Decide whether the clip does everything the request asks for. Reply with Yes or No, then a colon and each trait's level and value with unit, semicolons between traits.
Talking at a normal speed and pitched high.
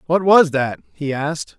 No: average, 190 wpm; medium, 155 Hz